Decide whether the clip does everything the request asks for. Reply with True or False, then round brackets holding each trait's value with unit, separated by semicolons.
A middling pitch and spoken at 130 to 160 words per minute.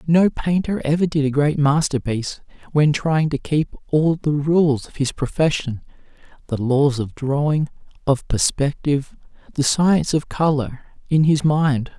True (145 Hz; 150 wpm)